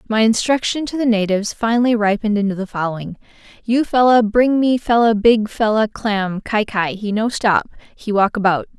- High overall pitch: Yes, high, 220 Hz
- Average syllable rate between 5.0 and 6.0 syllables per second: Yes, 5.3 syllables/s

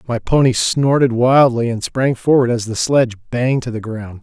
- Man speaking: Yes, male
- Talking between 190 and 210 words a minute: Yes, average, 200 wpm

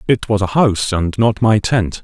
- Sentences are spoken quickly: Yes, fast, 235 wpm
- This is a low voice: Yes, low, 105 Hz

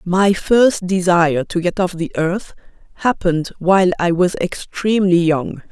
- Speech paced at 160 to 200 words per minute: No, average, 145 wpm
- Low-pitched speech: No, medium, 180 Hz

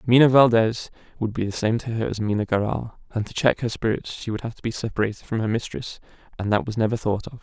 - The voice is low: Yes, low, 115 Hz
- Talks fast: Yes, fast, 250 wpm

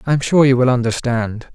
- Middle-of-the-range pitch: No, low, 125 Hz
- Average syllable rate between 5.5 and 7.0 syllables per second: Yes, 5.6 syllables/s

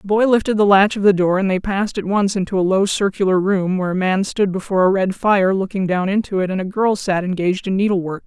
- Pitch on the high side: Yes, high, 195 Hz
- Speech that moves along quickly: Yes, fast, 270 wpm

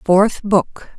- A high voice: Yes, high, 195 Hz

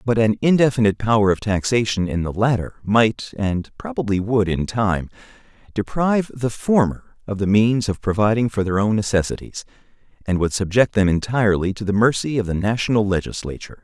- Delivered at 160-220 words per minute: Yes, average, 170 wpm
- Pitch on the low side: Yes, low, 110 Hz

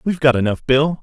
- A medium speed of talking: No, fast, 235 wpm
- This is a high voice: No, medium, 140 Hz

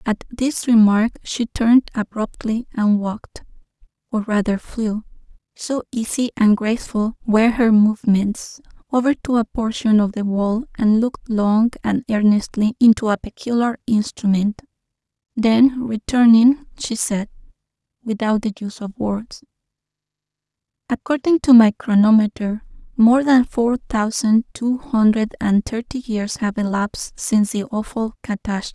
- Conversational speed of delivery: No, slow, 125 wpm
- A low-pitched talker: No, high, 225 Hz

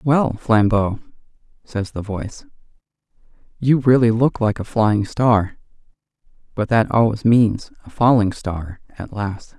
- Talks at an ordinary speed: No, slow, 130 wpm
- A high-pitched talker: No, low, 110 Hz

